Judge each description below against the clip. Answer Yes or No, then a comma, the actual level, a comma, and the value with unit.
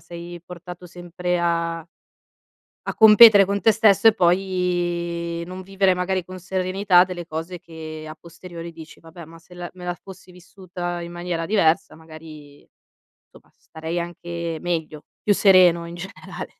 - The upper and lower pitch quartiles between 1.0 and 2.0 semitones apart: Yes, narrow, 1.7 semitones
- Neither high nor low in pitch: Yes, medium, 175 Hz